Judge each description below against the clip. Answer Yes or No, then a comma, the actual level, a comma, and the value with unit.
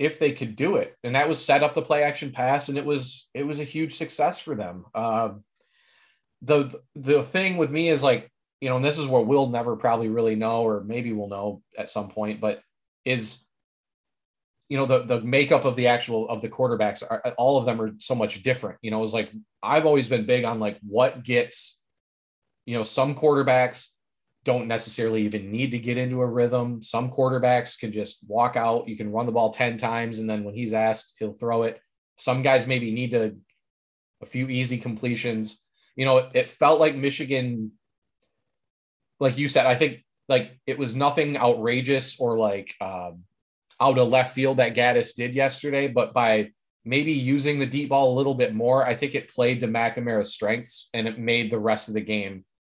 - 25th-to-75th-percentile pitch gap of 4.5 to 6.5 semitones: No, average, 3.5 semitones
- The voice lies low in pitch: Yes, low, 125 Hz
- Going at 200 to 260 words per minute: Yes, fast, 205 wpm